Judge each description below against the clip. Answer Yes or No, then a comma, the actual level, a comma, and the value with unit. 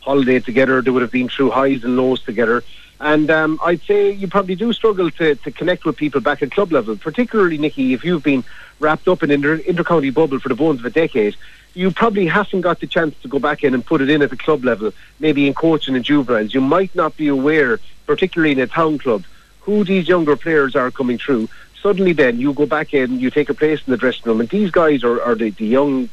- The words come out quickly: Yes, fast, 250 wpm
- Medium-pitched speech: Yes, medium, 150 Hz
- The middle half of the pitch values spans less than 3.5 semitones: No, average, 4.2 semitones